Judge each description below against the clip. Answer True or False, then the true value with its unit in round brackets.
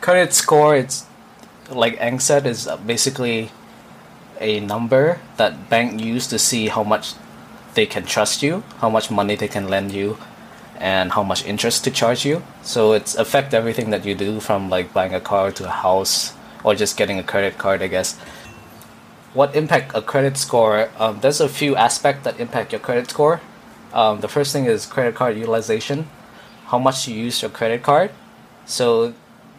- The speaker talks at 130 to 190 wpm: True (175 wpm)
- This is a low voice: True (115 Hz)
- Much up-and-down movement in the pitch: False (4.1 semitones)